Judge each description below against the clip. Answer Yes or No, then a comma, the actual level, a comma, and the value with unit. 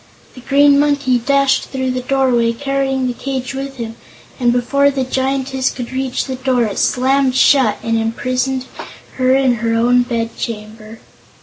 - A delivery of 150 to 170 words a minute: Yes, average, 165 wpm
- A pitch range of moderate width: No, narrow, 2.1 semitones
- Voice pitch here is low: No, very high, 255 Hz